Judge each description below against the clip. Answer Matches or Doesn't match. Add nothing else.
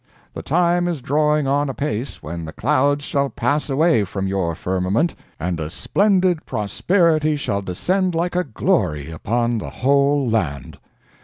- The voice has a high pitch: Doesn't match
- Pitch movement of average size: Doesn't match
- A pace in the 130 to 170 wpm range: Matches